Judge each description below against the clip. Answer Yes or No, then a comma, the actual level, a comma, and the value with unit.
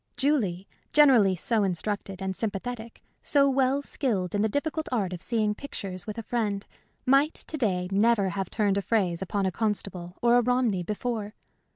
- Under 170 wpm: No, average, 175 wpm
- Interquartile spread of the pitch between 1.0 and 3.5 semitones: No, average, 4.4 semitones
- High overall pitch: Yes, high, 210 Hz